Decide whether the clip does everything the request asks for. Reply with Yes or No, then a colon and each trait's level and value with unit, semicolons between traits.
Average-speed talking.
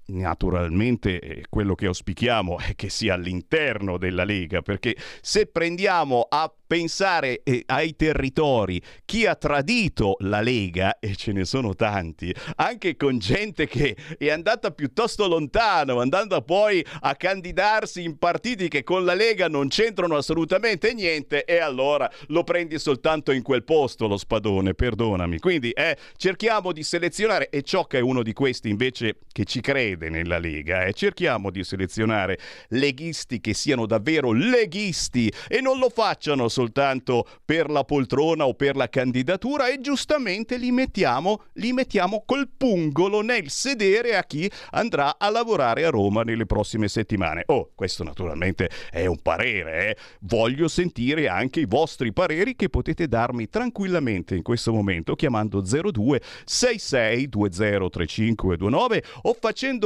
Yes: average, 150 wpm